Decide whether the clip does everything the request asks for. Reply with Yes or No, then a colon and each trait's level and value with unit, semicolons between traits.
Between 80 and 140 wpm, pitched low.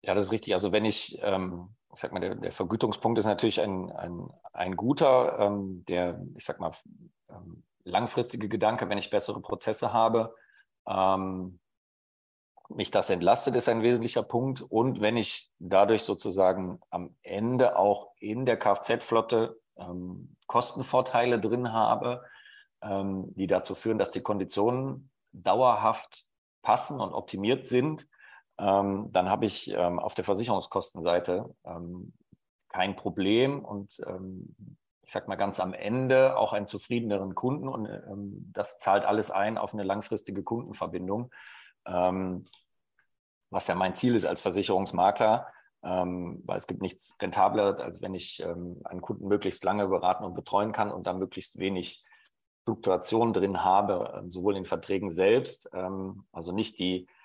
No: average, 150 wpm; low, 100 Hz